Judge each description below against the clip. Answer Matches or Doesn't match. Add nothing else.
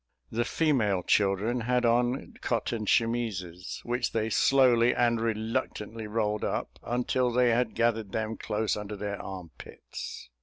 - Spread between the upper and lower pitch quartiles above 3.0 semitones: Doesn't match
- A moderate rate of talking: Doesn't match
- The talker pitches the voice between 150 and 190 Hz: Doesn't match